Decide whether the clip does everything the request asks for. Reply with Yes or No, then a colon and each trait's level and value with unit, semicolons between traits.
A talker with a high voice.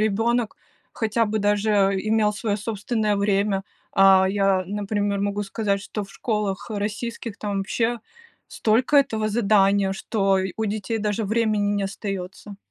Yes: high, 205 Hz